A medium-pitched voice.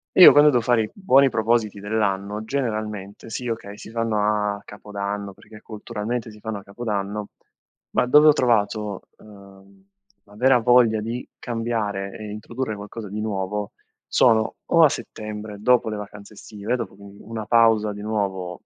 No: low, 105 Hz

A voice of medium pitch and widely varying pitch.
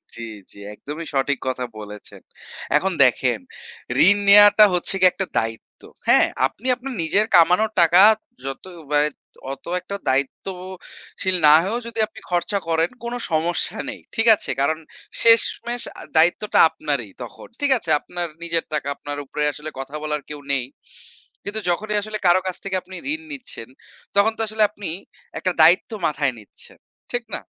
Yes: medium, 175 Hz; wide, 5.9 semitones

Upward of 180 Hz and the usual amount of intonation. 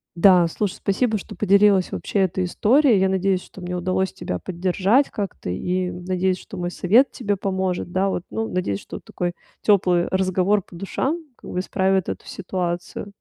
No: high, 190 Hz; narrow, 2.0 semitones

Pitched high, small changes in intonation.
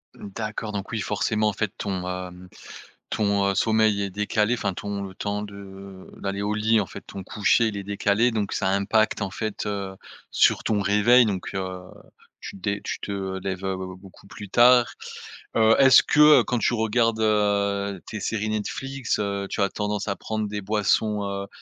No: low, 105 Hz; narrow, 1.7 semitones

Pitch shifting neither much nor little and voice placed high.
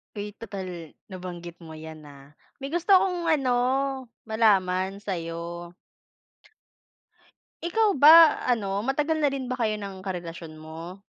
No: wide, 7.9 semitones; high, 195 Hz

